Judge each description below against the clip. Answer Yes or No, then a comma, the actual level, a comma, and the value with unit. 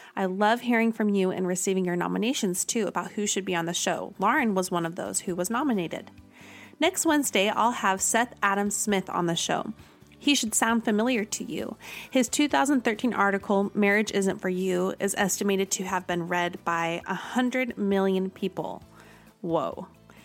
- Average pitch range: Yes, average, 3.6 semitones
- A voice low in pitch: No, high, 200 Hz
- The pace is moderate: Yes, average, 175 wpm